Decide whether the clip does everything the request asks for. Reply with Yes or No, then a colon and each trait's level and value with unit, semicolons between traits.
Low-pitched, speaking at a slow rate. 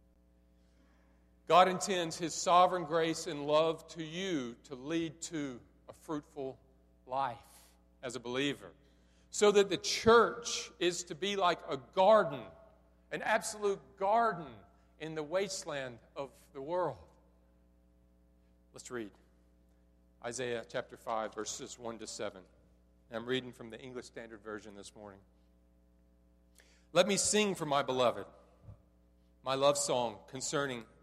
Yes: low, 120 Hz; slow, 125 wpm